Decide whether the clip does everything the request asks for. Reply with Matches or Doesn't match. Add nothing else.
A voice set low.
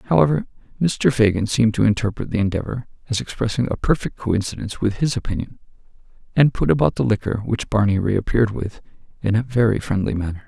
Matches